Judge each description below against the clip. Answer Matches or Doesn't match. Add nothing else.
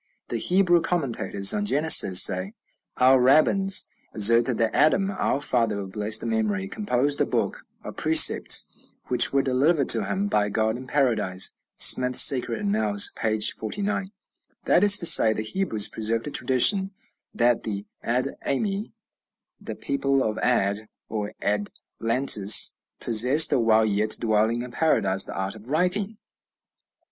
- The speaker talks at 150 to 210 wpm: Doesn't match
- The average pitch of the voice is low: Matches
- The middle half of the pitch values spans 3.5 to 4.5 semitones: Doesn't match